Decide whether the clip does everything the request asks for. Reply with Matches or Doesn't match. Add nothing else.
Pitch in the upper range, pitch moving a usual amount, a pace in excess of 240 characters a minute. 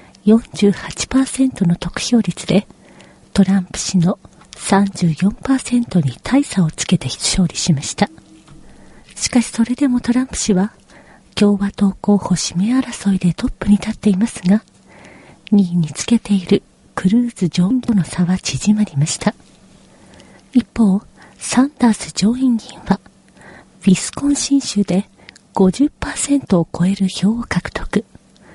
Doesn't match